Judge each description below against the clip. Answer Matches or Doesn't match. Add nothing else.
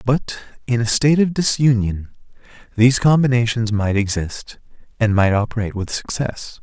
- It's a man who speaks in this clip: Matches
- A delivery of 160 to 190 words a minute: Doesn't match